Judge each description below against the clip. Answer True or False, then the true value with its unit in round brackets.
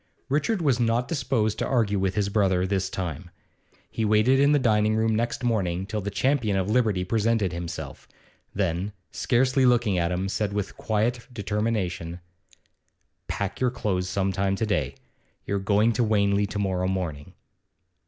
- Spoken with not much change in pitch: False (3.5 semitones)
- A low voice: True (105 Hz)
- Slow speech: False (165 wpm)